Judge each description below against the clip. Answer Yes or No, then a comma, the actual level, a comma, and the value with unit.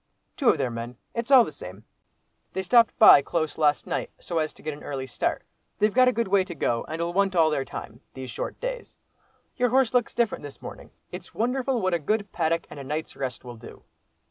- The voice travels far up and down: Yes, wide, 8.8 semitones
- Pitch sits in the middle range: Yes, medium, 170 Hz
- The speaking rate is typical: No, fast, 220 wpm